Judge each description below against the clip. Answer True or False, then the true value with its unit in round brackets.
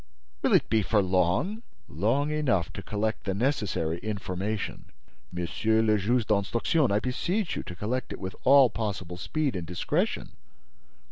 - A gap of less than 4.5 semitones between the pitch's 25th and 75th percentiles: False (5.6 semitones)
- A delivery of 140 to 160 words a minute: True (150 wpm)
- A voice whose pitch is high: False (110 Hz)